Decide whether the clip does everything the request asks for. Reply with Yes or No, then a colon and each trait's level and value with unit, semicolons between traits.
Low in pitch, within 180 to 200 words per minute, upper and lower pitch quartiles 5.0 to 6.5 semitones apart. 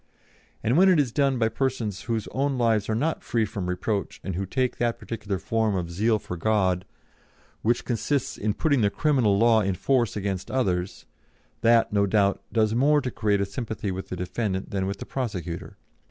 No: low, 110 Hz; average, 195 wpm; average, 4.0 semitones